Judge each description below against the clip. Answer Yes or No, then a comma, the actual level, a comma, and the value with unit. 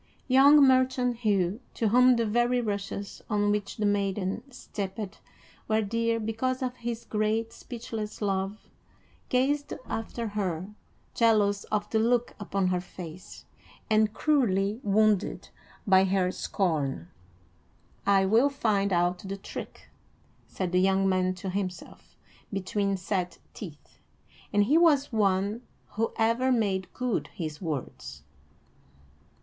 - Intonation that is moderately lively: Yes, average, 3.3 semitones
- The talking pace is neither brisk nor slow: No, slow, 125 wpm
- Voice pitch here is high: Yes, high, 205 Hz